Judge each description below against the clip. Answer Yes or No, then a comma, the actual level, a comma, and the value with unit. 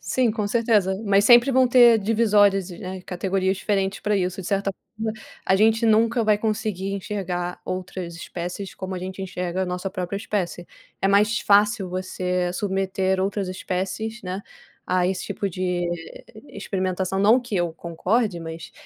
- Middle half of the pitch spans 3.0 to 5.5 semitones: No, narrow, 2.5 semitones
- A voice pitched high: Yes, high, 195 Hz